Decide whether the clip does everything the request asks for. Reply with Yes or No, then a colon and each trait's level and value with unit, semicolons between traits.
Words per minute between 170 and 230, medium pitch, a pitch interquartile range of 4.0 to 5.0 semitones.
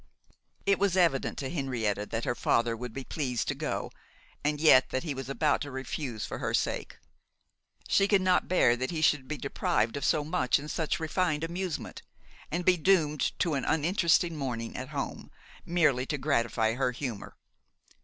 Yes: average, 180 wpm; medium, 145 Hz; average, 4.6 semitones